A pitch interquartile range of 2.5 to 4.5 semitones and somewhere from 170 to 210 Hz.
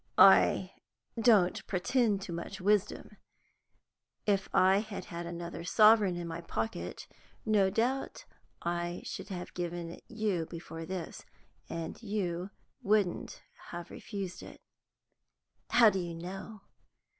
Yes: average, 3.4 semitones; medium, 185 Hz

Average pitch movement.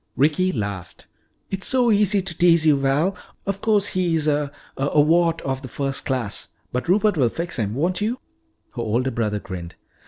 No: wide, 6.4 semitones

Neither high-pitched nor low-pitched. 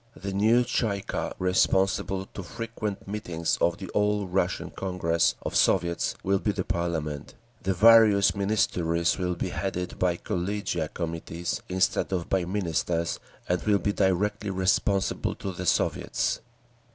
No: very low, 95 Hz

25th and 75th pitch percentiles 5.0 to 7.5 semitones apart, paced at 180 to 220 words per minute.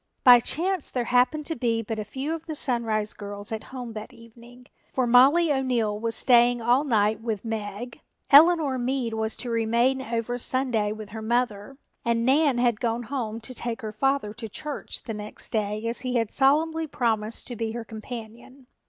No: average, 3.0 semitones; average, 190 wpm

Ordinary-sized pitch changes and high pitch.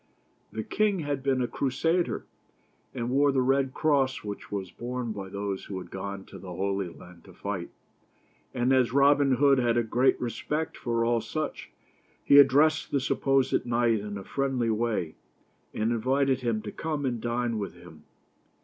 No: average, 5.0 semitones; low, 120 Hz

